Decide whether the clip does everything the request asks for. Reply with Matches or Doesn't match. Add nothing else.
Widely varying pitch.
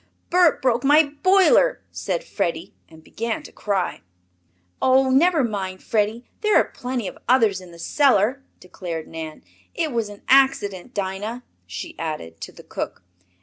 Matches